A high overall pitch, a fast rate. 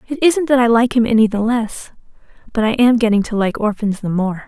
Yes: high, 230 Hz; fast, 240 wpm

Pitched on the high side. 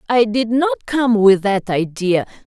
Yes: high, 215 Hz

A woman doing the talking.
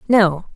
Yes: female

